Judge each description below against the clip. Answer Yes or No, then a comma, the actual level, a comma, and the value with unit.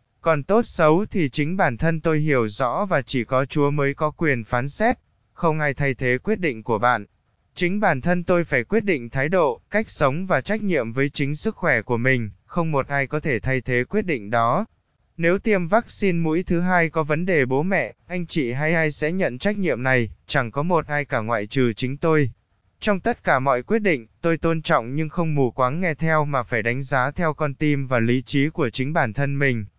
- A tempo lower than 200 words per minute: No, average, 235 wpm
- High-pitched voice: No, medium, 150 Hz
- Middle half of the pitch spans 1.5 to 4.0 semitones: No, average, 5.2 semitones